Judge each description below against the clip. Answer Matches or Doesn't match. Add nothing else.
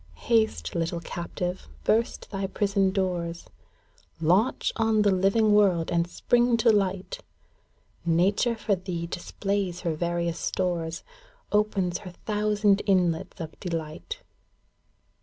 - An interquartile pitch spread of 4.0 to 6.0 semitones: Doesn't match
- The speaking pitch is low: Doesn't match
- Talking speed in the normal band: Doesn't match